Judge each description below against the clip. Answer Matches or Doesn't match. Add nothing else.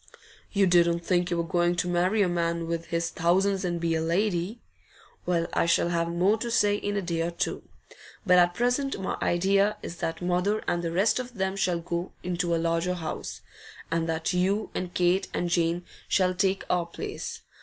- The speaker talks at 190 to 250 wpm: Matches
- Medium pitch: Matches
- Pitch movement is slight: Matches